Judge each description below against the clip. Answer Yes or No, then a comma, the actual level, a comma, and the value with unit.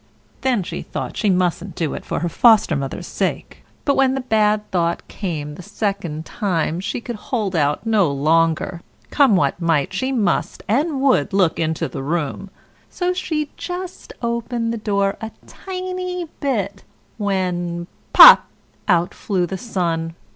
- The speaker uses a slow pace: No, average, 155 wpm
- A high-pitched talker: Yes, high, 200 Hz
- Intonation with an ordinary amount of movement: No, wide, 6.0 semitones